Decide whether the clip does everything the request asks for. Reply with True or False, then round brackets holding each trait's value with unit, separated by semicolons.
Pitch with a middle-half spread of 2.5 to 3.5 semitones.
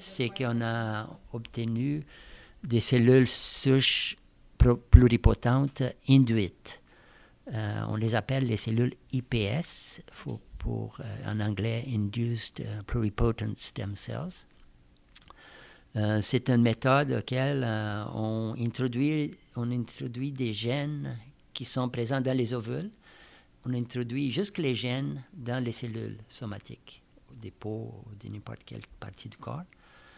True (2.9 semitones)